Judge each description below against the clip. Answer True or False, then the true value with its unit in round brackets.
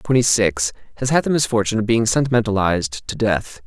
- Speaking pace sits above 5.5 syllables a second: True (6.1 syllables/s)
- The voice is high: False (110 Hz)